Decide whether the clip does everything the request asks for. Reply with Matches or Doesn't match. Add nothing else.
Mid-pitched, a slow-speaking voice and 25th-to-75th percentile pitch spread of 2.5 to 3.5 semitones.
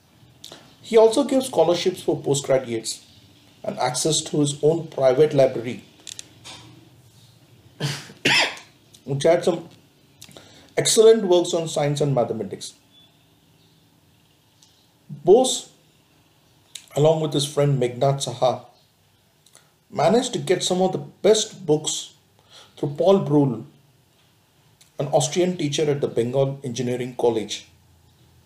Doesn't match